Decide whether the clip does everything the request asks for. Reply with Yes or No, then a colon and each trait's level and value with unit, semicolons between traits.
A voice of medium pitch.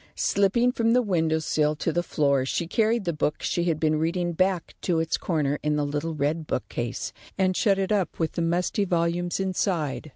Yes: medium, 170 Hz